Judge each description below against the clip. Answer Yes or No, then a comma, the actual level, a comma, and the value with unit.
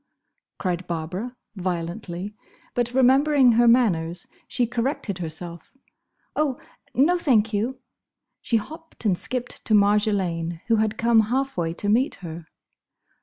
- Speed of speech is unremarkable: No, slow, 125 wpm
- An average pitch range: No, wide, 6.0 semitones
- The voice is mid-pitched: No, high, 215 Hz